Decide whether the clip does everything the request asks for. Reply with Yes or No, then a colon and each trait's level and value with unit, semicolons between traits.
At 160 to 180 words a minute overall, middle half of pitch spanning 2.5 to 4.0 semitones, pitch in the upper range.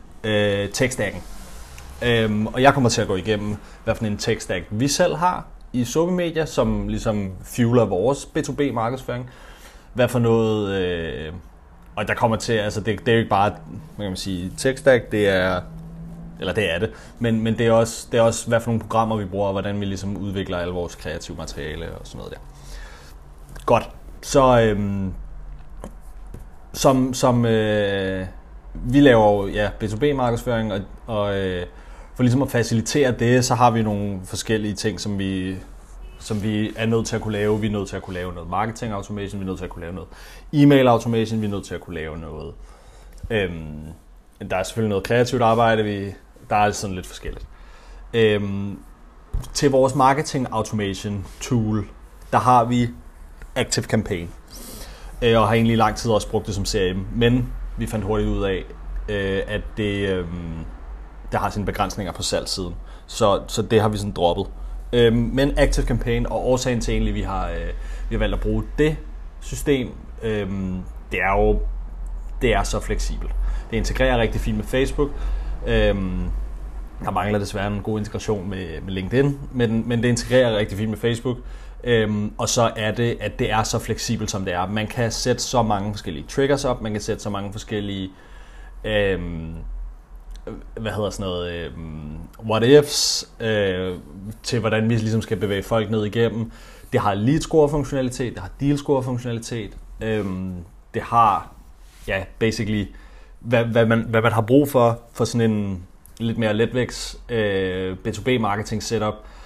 No: average, 175 wpm; average, 3.7 semitones; low, 105 Hz